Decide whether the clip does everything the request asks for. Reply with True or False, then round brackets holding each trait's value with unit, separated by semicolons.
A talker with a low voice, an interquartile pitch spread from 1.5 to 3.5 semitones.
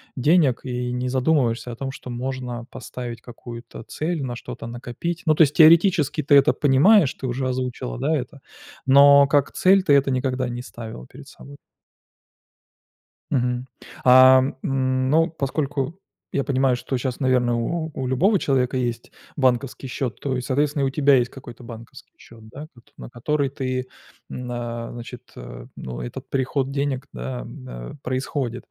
True (130 Hz; 2.6 semitones)